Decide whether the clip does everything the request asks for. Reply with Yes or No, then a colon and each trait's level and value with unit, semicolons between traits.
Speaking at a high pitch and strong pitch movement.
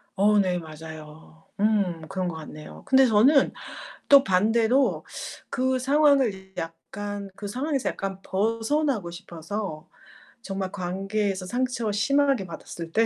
Yes: high, 205 Hz; wide, 5.7 semitones